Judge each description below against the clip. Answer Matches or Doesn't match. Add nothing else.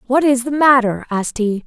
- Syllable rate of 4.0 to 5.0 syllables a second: Doesn't match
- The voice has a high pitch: Matches